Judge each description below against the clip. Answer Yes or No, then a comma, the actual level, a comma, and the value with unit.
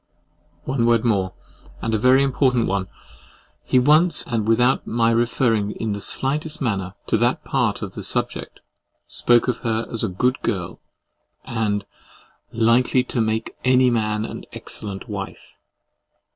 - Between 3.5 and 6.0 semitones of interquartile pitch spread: No, average, 2.9 semitones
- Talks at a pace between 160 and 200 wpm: No, average, 150 wpm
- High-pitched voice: No, low, 115 Hz